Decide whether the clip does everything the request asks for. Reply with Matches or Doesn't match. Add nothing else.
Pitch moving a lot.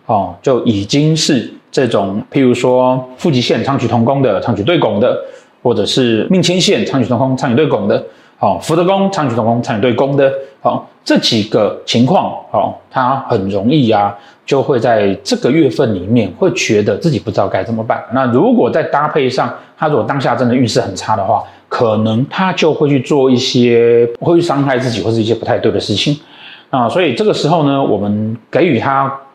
Doesn't match